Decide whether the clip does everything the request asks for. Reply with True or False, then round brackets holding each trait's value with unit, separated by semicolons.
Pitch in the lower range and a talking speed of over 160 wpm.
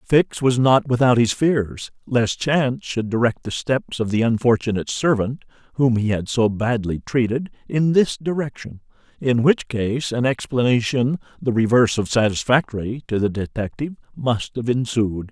False (120 Hz; 155 wpm)